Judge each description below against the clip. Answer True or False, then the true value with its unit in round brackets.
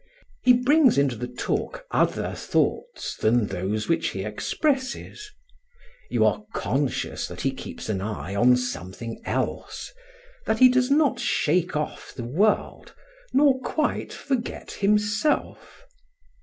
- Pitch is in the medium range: True (175 Hz)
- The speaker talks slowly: True (130 wpm)